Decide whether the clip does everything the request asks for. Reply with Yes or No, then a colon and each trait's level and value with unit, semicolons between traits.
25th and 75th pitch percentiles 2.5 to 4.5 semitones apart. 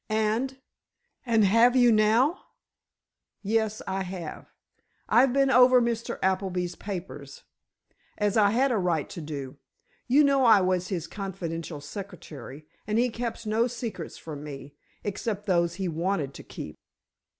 No: average, 5.1 semitones